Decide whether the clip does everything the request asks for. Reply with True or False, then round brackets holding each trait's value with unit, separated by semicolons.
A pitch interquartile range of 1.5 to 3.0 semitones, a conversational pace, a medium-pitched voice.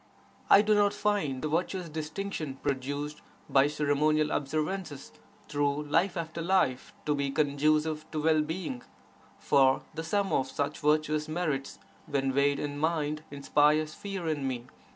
True (2.5 semitones; 145 wpm; 150 Hz)